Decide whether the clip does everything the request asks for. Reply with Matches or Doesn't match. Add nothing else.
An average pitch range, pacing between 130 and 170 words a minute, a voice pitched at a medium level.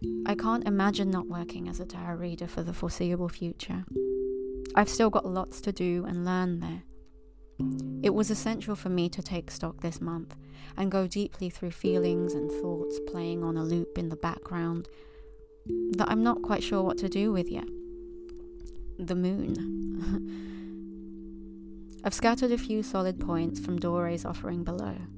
Doesn't match